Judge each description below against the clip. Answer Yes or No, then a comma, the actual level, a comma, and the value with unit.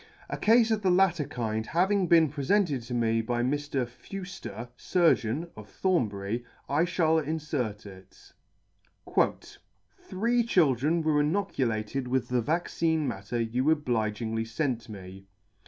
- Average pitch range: No, wide, 7.0 semitones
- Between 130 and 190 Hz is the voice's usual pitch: Yes, low, 135 Hz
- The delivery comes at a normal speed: No, slow, 130 wpm